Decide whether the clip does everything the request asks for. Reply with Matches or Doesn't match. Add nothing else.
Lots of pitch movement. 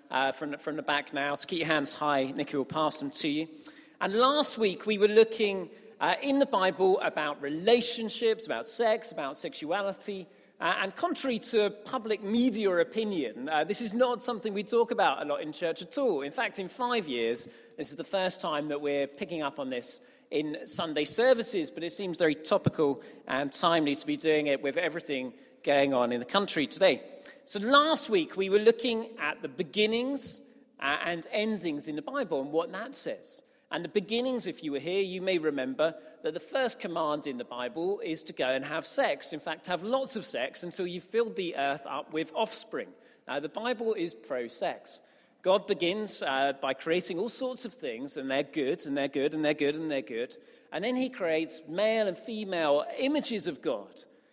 Matches